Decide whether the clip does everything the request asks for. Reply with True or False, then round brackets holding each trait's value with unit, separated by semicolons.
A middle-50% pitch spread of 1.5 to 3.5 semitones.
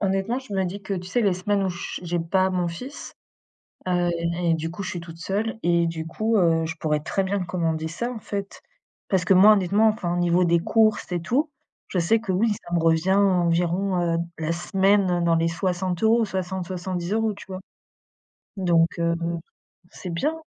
True (2.8 semitones)